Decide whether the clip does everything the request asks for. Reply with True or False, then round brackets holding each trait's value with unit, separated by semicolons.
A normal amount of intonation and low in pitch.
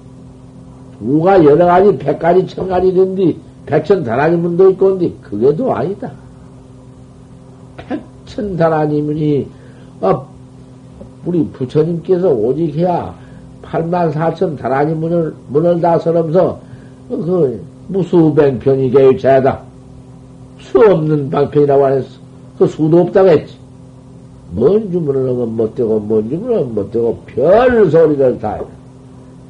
False (4.8 semitones; 150 Hz)